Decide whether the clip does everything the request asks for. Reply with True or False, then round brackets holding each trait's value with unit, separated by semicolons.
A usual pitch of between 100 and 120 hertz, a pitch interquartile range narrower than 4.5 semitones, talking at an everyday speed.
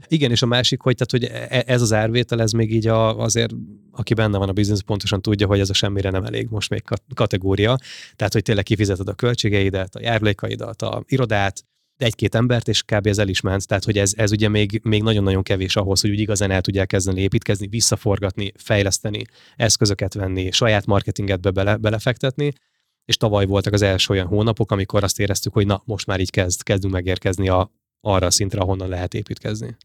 False (105 Hz; 2.5 semitones; 200 wpm)